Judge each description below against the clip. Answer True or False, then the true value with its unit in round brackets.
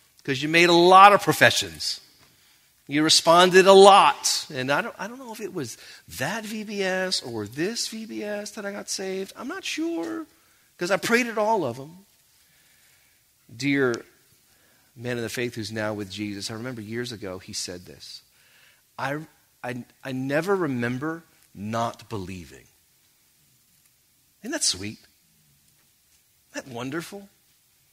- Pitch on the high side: False (140 Hz)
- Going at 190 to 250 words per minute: False (145 wpm)